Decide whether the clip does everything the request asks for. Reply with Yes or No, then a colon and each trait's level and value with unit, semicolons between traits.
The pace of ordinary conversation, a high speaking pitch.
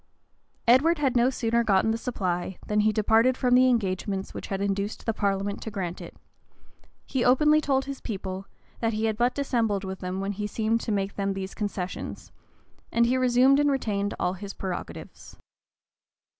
Yes: average, 180 wpm; high, 215 Hz